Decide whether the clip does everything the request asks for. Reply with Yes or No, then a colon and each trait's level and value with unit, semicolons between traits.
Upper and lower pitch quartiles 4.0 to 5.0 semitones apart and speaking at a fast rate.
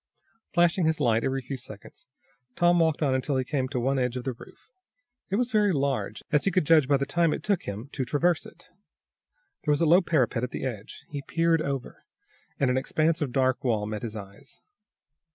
Yes: average, 4.6 semitones; fast, 215 wpm